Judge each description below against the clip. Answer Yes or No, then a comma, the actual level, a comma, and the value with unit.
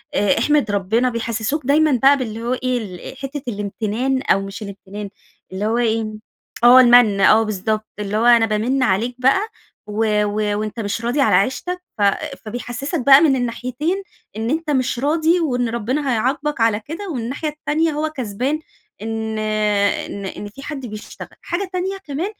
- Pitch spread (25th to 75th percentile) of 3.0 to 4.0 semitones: No, average, 4.8 semitones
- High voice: Yes, high, 240 Hz